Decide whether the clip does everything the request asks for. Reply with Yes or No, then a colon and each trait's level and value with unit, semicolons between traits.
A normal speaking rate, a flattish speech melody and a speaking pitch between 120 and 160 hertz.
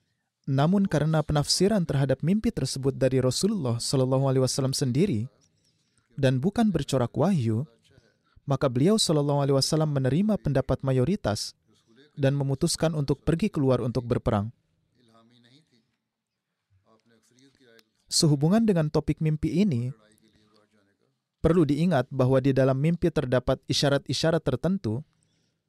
No: average, 105 wpm; average, 4.1 semitones; low, 135 Hz